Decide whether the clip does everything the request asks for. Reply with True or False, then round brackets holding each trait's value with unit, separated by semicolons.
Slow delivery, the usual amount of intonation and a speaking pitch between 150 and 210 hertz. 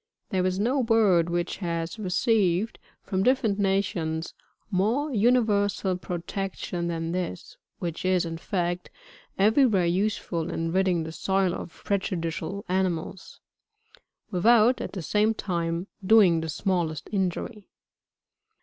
True (125 wpm; 3.4 semitones; 185 Hz)